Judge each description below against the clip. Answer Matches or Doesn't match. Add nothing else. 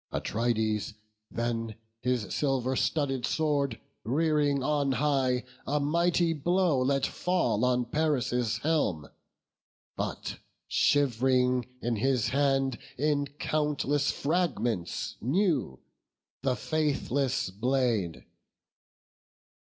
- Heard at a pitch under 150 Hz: Matches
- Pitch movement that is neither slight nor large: Matches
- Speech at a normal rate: Doesn't match